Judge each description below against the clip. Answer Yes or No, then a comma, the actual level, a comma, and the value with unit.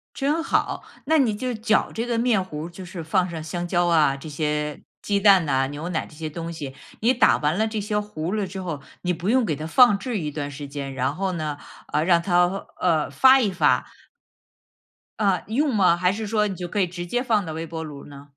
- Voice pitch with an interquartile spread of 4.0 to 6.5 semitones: Yes, average, 5.3 semitones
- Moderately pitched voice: Yes, medium, 180 Hz